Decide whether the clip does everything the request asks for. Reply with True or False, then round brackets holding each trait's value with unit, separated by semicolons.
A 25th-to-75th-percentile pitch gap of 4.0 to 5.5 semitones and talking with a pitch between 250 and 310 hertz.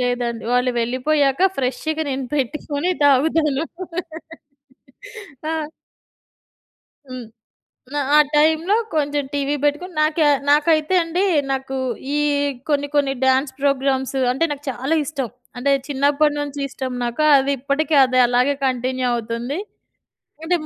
False (2.9 semitones; 280 Hz)